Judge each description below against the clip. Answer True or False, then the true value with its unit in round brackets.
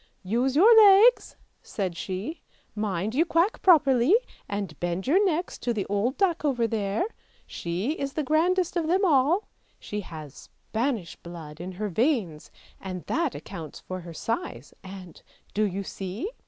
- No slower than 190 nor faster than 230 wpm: False (165 wpm)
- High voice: True (220 Hz)